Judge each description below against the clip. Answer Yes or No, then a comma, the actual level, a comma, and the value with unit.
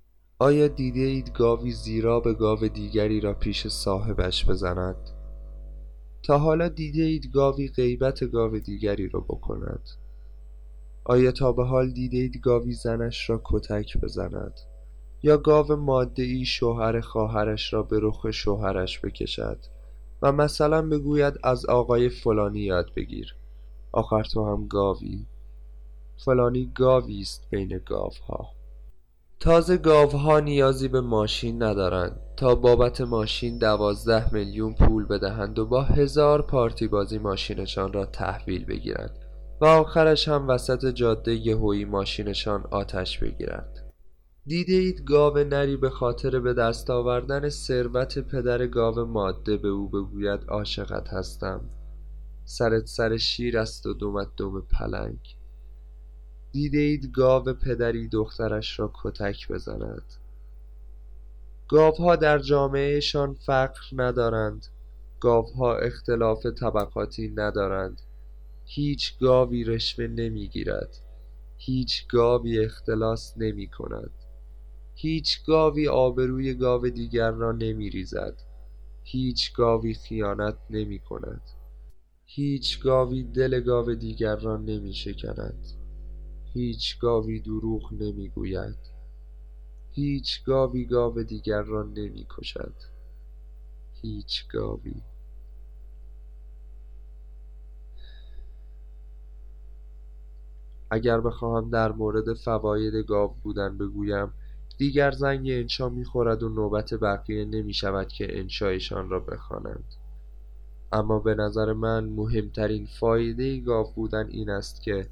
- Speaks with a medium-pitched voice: No, low, 110 Hz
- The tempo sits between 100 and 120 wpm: Yes, average, 110 wpm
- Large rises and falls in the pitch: Yes, wide, 7.9 semitones